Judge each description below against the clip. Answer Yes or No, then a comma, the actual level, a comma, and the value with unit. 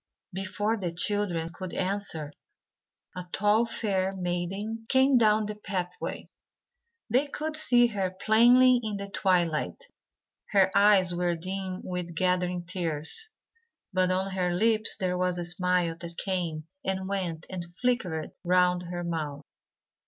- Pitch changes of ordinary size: Yes, average, 3.0 semitones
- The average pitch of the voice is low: No, medium, 185 Hz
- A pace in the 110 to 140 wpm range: Yes, slow, 135 wpm